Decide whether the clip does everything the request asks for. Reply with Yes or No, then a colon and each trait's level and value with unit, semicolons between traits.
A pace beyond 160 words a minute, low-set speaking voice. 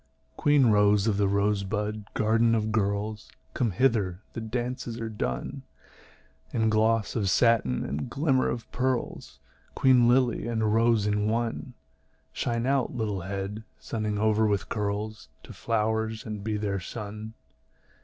No: average, 145 wpm; low, 110 Hz